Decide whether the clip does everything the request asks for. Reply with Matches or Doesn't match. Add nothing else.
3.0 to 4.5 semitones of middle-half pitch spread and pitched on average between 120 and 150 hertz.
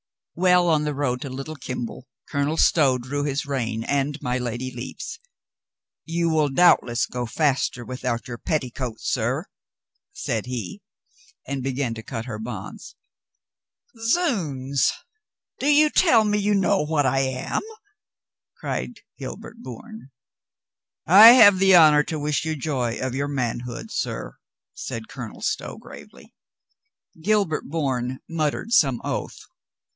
Doesn't match